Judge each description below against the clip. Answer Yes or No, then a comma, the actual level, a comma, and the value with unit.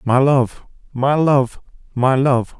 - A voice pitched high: No, low, 130 Hz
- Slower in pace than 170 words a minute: Yes, average, 140 wpm